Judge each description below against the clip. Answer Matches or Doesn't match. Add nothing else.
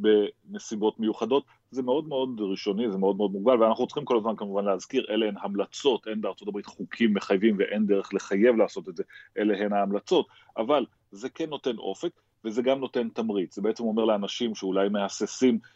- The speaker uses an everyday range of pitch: Matches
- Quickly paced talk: Matches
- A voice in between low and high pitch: Doesn't match